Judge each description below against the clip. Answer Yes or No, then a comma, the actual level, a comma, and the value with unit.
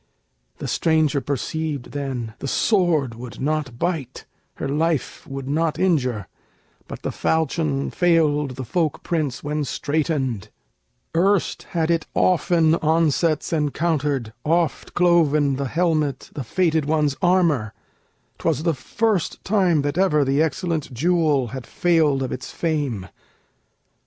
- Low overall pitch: No, medium, 150 Hz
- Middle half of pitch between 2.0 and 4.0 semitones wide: Yes, average, 3.4 semitones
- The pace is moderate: No, slow, 125 wpm